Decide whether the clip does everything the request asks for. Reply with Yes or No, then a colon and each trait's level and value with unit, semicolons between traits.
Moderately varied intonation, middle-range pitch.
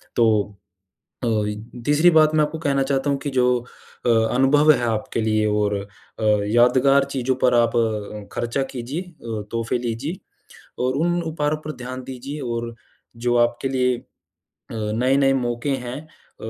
No: average, 3.2 semitones; low, 125 Hz